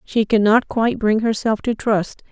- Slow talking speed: No, fast, 205 wpm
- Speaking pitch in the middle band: No, high, 220 Hz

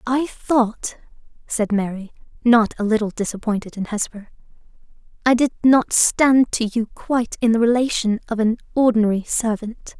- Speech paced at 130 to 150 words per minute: Yes, average, 145 wpm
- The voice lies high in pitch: Yes, high, 230 Hz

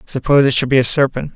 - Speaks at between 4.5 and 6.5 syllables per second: No, 7.4 syllables/s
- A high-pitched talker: No, low, 135 Hz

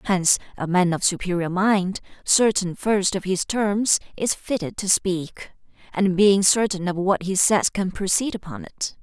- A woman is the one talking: Yes, female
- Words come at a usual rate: Yes, average, 175 wpm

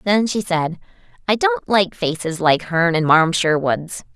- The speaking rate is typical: Yes, average, 175 wpm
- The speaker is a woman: Yes, female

